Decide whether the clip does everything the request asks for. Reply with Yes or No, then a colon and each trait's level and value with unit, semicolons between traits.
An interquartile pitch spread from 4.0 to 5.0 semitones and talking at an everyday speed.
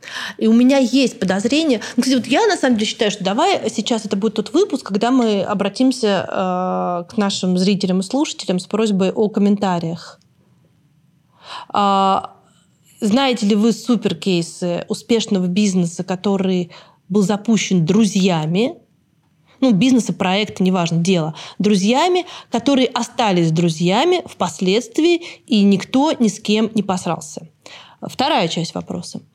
Yes: average, 4.3 semitones; average, 125 wpm